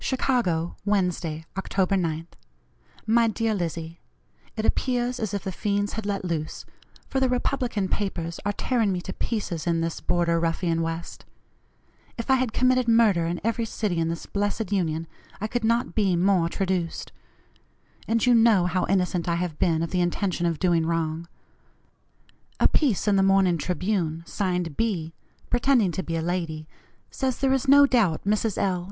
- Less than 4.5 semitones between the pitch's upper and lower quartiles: No, average, 4.9 semitones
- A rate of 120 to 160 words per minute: No, average, 170 wpm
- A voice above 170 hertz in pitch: Yes, high, 190 Hz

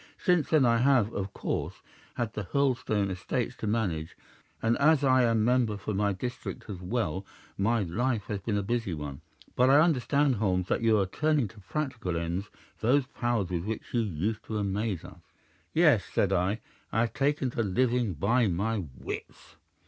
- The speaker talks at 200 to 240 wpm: No, average, 180 wpm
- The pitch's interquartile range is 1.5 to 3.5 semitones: No, average, 4.4 semitones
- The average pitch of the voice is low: Yes, low, 110 Hz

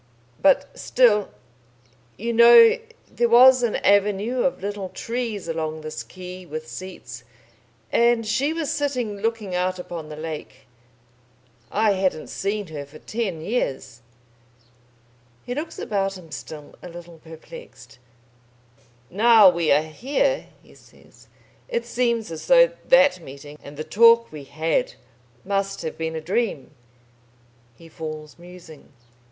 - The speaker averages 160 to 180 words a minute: No, slow, 135 wpm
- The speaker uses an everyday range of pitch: No, wide, 6.8 semitones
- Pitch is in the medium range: No, high, 195 Hz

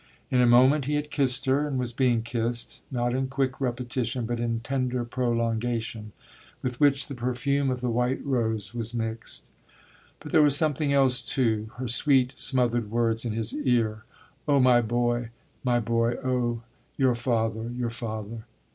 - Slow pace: No, average, 165 wpm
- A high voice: No, low, 120 Hz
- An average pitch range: No, narrow, 2.1 semitones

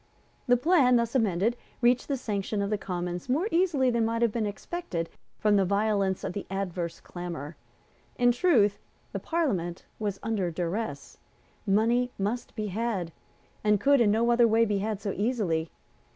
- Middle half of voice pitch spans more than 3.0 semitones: Yes, average, 3.9 semitones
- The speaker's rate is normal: Yes, average, 165 wpm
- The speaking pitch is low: No, high, 215 Hz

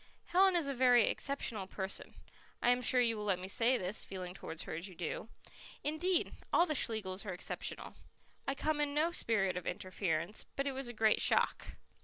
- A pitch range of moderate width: No, wide, 6.7 semitones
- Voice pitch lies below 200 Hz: No, high, 230 Hz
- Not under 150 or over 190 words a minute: No, average, 200 wpm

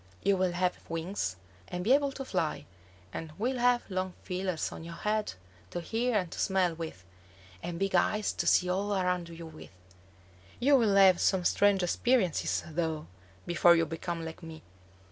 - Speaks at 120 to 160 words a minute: No, average, 175 wpm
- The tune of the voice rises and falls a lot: No, average, 3.5 semitones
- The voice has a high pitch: No, medium, 180 Hz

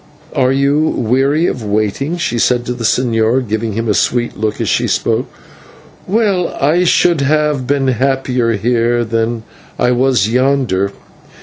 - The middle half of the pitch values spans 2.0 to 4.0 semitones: Yes, average, 3.3 semitones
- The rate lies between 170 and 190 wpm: No, average, 150 wpm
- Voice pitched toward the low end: Yes, low, 125 Hz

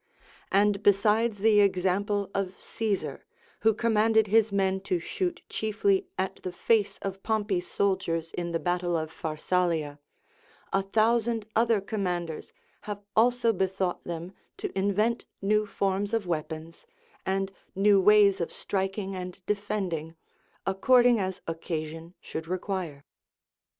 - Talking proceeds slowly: Yes, slow, 125 wpm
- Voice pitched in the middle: No, high, 195 Hz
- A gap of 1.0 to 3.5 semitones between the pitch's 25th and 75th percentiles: Yes, average, 3.1 semitones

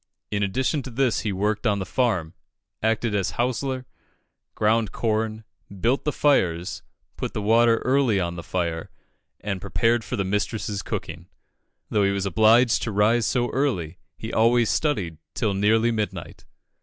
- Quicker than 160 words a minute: No, average, 155 wpm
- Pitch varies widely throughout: No, average, 3.4 semitones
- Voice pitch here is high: No, low, 110 Hz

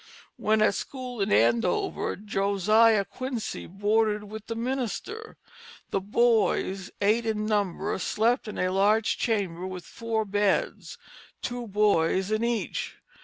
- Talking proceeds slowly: Yes, slow, 125 wpm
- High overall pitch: Yes, high, 210 Hz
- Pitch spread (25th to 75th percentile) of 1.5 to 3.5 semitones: Yes, narrow, 2.6 semitones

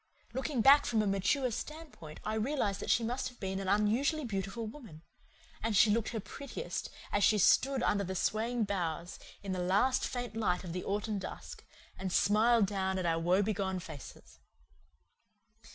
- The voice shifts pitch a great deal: No, average, 4.2 semitones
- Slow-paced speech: No, average, 170 wpm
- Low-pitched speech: No, high, 210 Hz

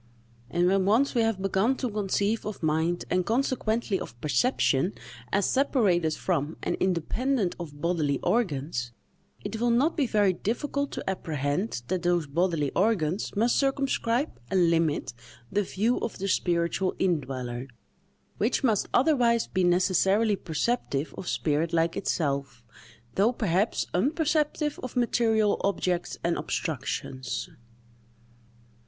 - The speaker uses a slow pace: Yes, slow, 130 wpm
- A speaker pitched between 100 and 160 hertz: No, high, 190 Hz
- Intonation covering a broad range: Yes, wide, 6.0 semitones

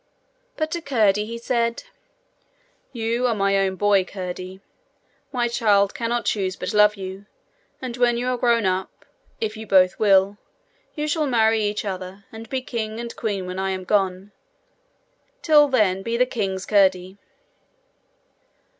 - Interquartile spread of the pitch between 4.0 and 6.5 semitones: No, average, 3.6 semitones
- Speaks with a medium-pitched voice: No, high, 210 Hz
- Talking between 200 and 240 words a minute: No, average, 155 wpm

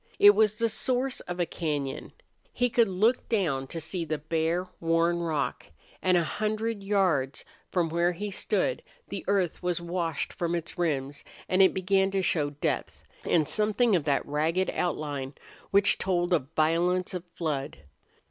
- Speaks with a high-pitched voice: No, medium, 175 Hz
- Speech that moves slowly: No, average, 165 wpm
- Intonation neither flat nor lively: Yes, average, 3.9 semitones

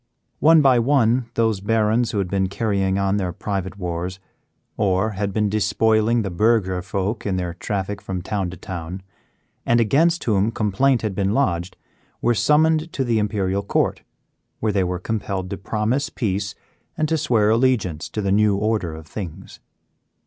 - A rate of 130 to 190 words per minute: Yes, average, 170 wpm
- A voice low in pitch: Yes, low, 105 Hz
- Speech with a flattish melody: No, average, 3.3 semitones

